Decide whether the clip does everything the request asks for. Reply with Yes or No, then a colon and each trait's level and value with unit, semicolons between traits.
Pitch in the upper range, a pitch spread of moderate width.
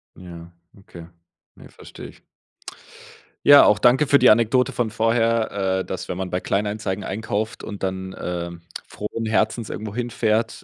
No: low, 105 Hz; average, 3.3 semitones